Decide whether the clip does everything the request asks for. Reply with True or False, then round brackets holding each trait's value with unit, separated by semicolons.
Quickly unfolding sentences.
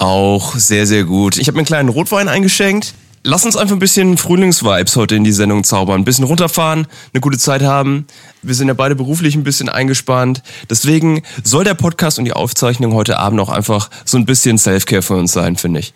True (215 wpm)